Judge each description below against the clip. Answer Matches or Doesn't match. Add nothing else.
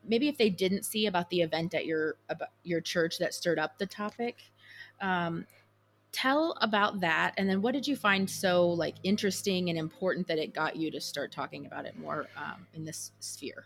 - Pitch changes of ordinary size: Matches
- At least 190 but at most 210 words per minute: Matches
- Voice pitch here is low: Doesn't match